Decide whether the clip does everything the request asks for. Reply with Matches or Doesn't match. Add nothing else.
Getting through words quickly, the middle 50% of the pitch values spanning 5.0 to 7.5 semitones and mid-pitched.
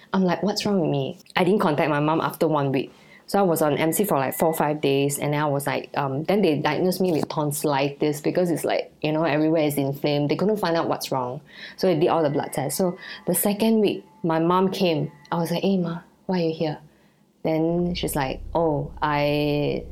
Doesn't match